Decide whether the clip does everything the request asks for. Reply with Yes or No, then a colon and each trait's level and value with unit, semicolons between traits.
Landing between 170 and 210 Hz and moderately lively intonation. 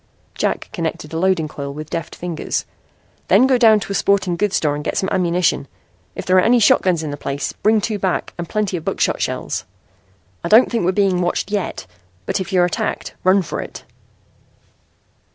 Yes: medium, 185 Hz; average, 3.5 semitones